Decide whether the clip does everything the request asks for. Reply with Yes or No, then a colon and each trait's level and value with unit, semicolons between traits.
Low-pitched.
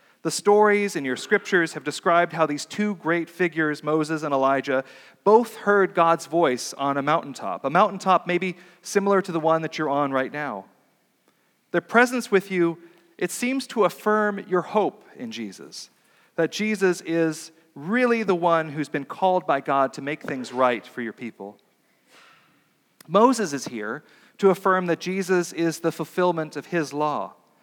No: medium, 170 Hz